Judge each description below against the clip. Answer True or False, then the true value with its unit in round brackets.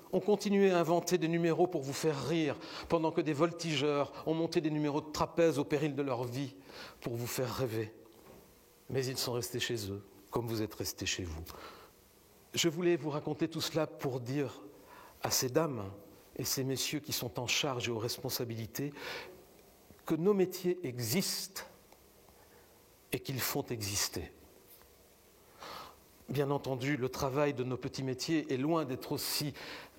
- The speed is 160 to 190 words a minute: True (165 wpm)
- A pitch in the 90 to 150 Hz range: True (140 Hz)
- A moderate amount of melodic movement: True (4.6 semitones)